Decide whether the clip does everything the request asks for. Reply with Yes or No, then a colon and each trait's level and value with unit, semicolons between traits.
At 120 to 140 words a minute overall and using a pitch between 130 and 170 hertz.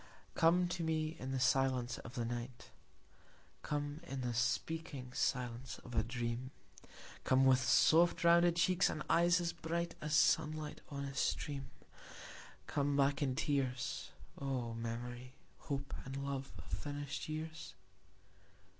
Yes: slow, 135 wpm; medium, 140 Hz